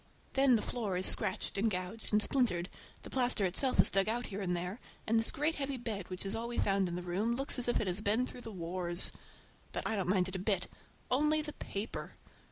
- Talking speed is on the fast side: Yes, fast, 235 wpm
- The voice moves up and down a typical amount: Yes, average, 4.7 semitones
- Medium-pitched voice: No, high, 210 Hz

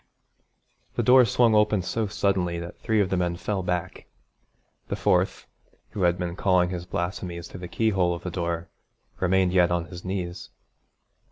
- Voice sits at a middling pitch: No, very low, 90 Hz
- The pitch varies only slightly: Yes, narrow, 1.9 semitones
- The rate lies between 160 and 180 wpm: Yes, average, 170 wpm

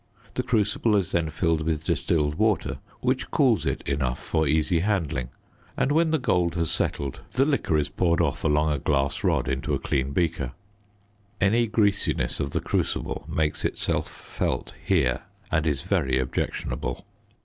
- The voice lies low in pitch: Yes, very low, 80 Hz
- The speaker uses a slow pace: No, average, 160 wpm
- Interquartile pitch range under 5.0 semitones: No, average, 5.3 semitones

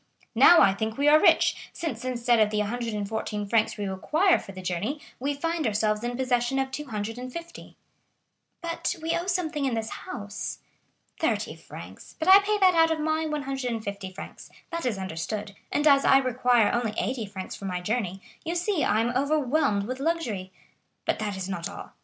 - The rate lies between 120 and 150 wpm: No, average, 175 wpm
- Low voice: No, high, 245 Hz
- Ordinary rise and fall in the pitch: No, wide, 6.6 semitones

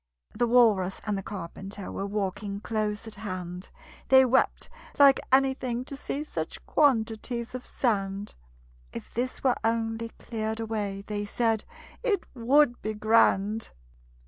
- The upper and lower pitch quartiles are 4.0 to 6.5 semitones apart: No, average, 3.3 semitones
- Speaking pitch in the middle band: No, high, 225 Hz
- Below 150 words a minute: Yes, slow, 135 wpm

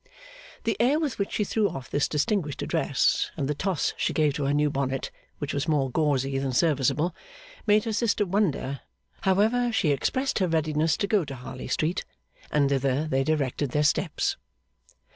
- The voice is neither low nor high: Yes, medium, 150 Hz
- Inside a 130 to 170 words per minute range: No, average, 180 wpm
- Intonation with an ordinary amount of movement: No, wide, 6.4 semitones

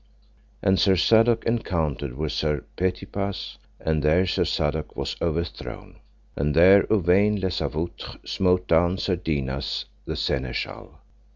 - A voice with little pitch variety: No, average, 4.0 semitones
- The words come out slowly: Yes, slow, 125 wpm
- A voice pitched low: Yes, very low, 85 Hz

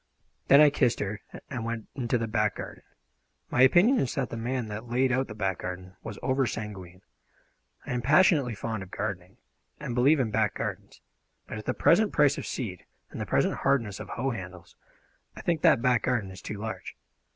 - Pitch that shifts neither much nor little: Yes, average, 4.3 semitones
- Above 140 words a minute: Yes, average, 200 wpm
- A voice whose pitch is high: No, low, 115 Hz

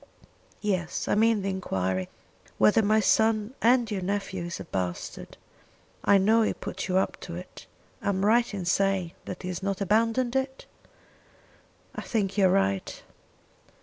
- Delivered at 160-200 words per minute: Yes, average, 165 wpm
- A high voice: Yes, high, 195 Hz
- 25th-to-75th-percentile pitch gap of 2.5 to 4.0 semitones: Yes, average, 3.4 semitones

